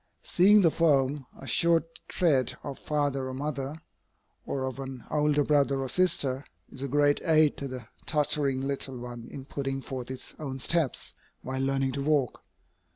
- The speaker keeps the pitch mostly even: Yes, narrow, 2.2 semitones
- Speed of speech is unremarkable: Yes, average, 160 wpm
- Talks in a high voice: No, medium, 140 Hz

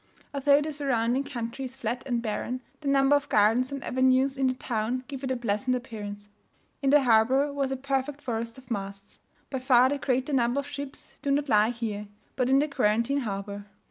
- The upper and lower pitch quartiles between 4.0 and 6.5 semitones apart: No, average, 3.2 semitones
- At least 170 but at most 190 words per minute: No, fast, 205 wpm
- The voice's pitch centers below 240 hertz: No, very high, 255 Hz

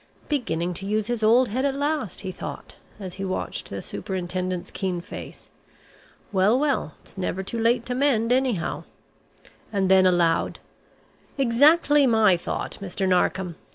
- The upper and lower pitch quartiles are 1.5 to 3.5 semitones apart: No, average, 5.3 semitones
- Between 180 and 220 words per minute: No, average, 150 wpm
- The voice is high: Yes, high, 205 Hz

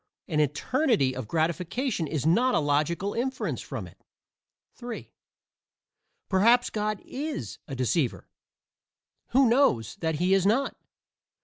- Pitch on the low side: No, high, 190 Hz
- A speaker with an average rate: No, slow, 120 wpm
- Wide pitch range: Yes, wide, 8.3 semitones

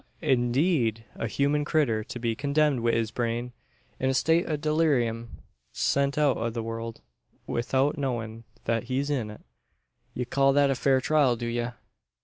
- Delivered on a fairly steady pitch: No, average, 3.6 semitones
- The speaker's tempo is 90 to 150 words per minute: No, average, 165 wpm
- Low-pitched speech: Yes, low, 125 Hz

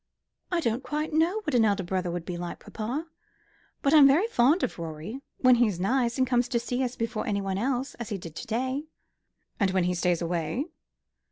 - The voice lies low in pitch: No, high, 235 Hz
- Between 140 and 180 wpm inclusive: No, fast, 205 wpm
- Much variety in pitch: Yes, wide, 6.2 semitones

